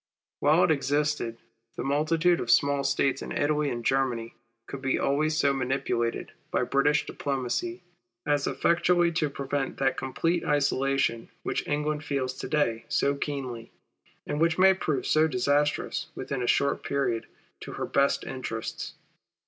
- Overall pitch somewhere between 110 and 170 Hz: Yes, medium, 140 Hz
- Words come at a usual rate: Yes, average, 150 wpm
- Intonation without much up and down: Yes, narrow, 2.2 semitones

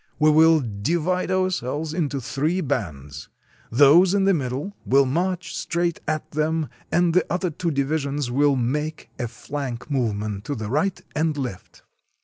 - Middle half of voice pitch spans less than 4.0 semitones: No, average, 4.8 semitones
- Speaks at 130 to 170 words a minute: Yes, average, 155 wpm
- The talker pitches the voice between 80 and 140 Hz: No, medium, 150 Hz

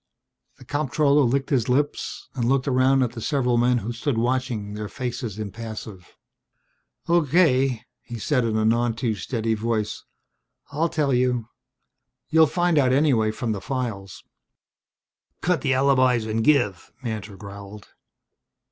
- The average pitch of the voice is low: Yes, low, 125 Hz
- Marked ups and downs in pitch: No, average, 3.7 semitones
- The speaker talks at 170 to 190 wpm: No, average, 140 wpm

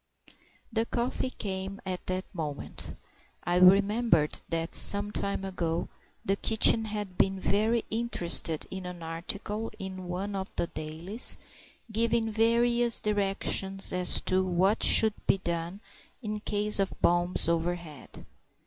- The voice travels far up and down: No, average, 3.2 semitones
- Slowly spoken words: Yes, slow, 130 wpm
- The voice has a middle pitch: No, high, 195 Hz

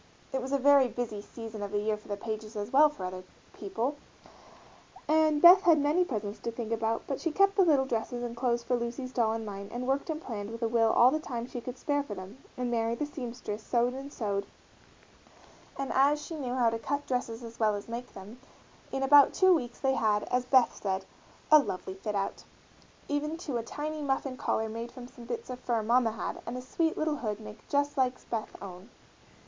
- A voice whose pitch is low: No, high, 245 Hz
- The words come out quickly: Yes, fast, 230 wpm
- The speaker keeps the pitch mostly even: No, average, 4.2 semitones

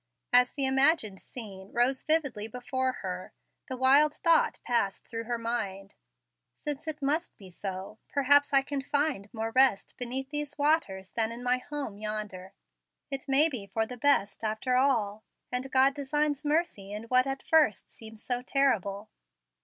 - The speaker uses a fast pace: No, average, 160 wpm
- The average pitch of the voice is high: Yes, very high, 250 Hz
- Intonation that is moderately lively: Yes, average, 4.7 semitones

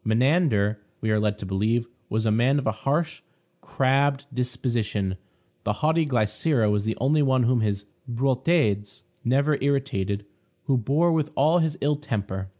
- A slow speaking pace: No, average, 155 wpm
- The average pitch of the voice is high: No, low, 125 Hz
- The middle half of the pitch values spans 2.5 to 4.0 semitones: No, average, 5.1 semitones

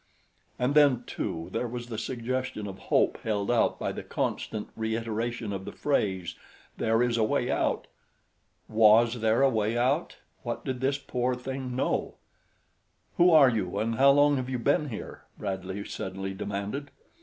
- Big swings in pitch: No, average, 3.5 semitones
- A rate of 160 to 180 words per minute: Yes, average, 165 wpm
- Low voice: Yes, low, 120 Hz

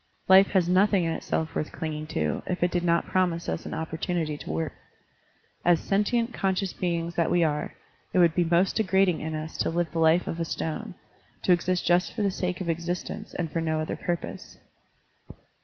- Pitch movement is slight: Yes, narrow, 2.2 semitones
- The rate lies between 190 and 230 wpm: Yes, average, 200 wpm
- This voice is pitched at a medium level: Yes, medium, 170 Hz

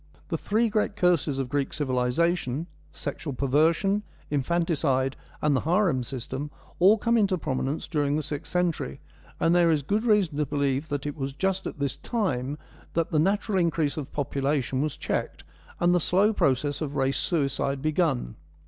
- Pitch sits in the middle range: Yes, medium, 150 Hz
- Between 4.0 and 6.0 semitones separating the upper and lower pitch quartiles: Yes, average, 4.3 semitones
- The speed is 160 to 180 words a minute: Yes, average, 175 wpm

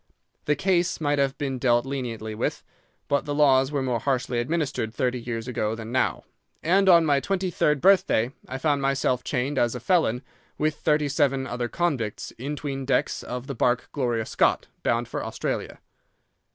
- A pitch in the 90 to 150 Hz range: Yes, low, 135 Hz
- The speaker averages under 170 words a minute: No, average, 180 wpm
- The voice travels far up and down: No, average, 3.4 semitones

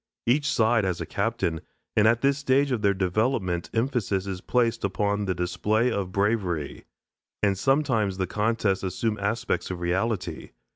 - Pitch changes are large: No, average, 3.7 semitones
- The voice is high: No, low, 105 Hz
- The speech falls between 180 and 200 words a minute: No, average, 155 wpm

